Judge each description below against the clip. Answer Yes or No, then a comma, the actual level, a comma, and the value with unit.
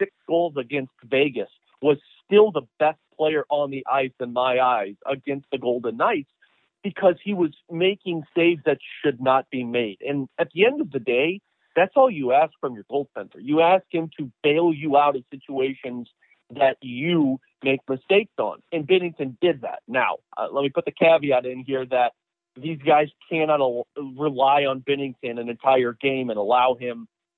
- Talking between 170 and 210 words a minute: Yes, average, 185 wpm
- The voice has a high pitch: No, medium, 140 Hz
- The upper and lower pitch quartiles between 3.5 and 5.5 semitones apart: Yes, average, 4.2 semitones